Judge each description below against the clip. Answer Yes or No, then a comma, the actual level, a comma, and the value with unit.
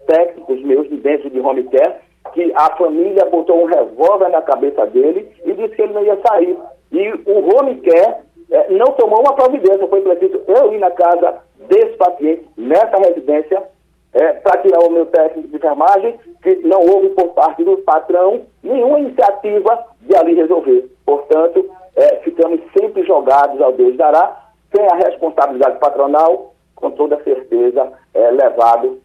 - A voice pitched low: No, high, 200 Hz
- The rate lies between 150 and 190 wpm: Yes, average, 165 wpm